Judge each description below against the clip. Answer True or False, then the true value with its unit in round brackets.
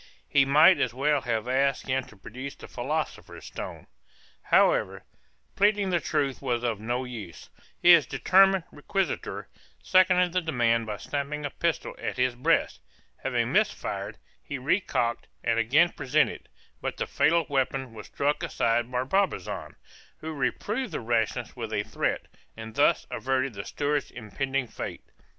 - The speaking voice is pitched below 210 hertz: True (135 Hz)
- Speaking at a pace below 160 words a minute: True (150 wpm)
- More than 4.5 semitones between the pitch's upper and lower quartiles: True (4.9 semitones)